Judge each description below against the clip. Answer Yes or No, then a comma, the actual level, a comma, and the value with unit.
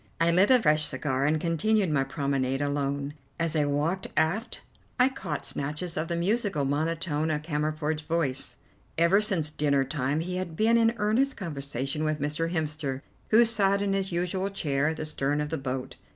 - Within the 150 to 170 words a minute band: No, average, 180 wpm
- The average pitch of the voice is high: No, medium, 155 Hz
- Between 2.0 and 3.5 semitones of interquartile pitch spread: No, average, 4.4 semitones